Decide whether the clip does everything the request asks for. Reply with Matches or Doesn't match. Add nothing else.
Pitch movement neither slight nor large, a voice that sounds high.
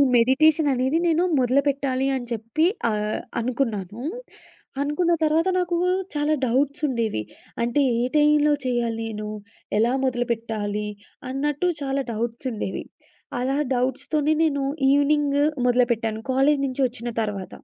Matches